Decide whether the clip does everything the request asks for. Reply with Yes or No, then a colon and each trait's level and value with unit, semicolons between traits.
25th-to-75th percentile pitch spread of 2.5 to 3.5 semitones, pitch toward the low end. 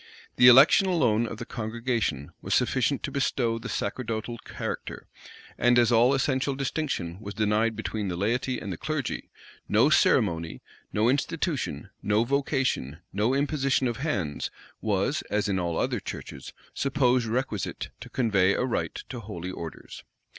No: average, 4.4 semitones; low, 115 Hz